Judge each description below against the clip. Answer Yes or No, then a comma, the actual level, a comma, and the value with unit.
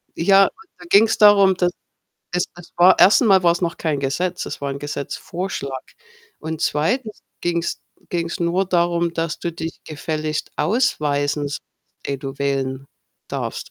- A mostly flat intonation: No, average, 3.8 semitones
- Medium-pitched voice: Yes, medium, 170 Hz